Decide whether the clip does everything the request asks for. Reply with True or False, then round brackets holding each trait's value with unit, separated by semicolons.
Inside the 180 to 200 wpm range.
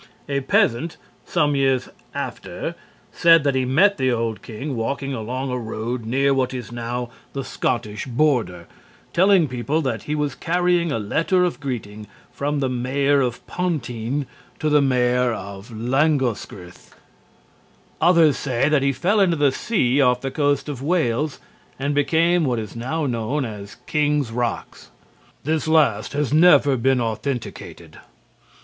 False (150 wpm)